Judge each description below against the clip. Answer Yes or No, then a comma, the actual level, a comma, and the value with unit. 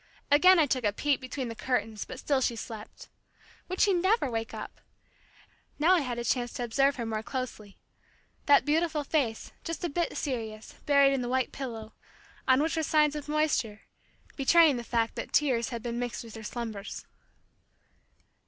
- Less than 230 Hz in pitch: No, very high, 260 Hz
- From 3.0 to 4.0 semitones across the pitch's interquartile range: No, average, 4.5 semitones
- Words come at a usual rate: Yes, average, 180 wpm